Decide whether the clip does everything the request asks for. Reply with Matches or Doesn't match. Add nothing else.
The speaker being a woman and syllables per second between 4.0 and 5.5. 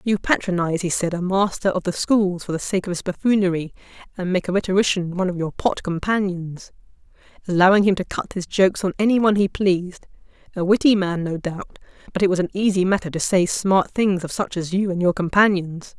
Doesn't match